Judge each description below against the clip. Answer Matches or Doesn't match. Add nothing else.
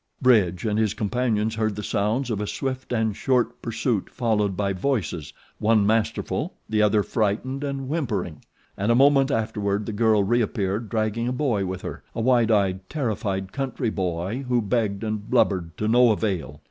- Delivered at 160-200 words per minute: Matches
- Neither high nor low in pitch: Doesn't match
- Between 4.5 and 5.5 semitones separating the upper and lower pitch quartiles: Doesn't match